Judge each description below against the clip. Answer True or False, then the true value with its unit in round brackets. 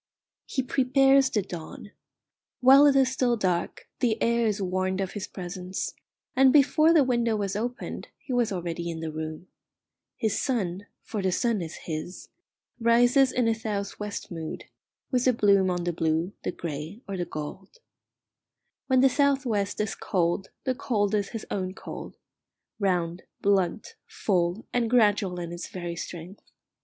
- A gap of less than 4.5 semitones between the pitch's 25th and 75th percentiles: False (5.4 semitones)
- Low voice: False (200 Hz)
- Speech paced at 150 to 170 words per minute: True (165 wpm)